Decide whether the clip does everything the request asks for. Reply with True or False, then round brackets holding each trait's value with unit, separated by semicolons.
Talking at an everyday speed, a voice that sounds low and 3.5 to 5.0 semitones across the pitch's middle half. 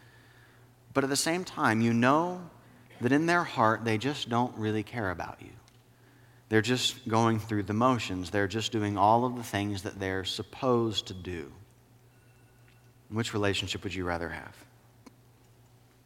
False (160 wpm; 120 Hz; 2.6 semitones)